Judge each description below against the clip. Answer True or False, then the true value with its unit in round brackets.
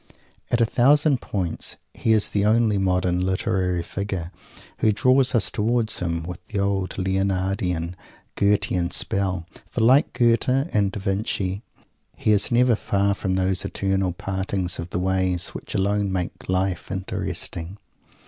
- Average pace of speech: True (145 wpm)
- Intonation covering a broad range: False (2.7 semitones)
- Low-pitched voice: True (95 Hz)